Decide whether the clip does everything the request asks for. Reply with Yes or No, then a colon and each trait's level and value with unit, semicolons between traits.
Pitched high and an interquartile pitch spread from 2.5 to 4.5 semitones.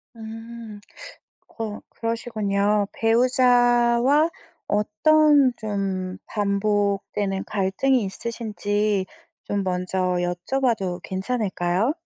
Yes: high, 210 Hz; average, 3.4 semitones